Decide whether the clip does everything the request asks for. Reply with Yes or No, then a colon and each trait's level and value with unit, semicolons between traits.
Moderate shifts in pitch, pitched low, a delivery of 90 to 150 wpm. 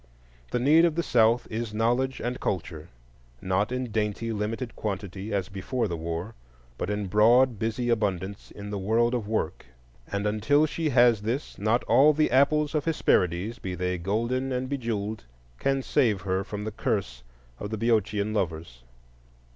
No: average, 4.1 semitones; low, 110 Hz; average, 165 wpm